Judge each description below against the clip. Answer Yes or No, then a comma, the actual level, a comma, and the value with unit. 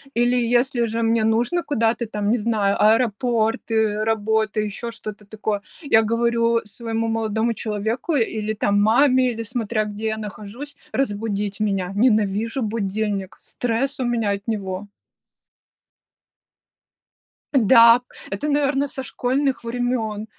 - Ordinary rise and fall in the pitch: No, narrow, 2.3 semitones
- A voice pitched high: Yes, high, 225 Hz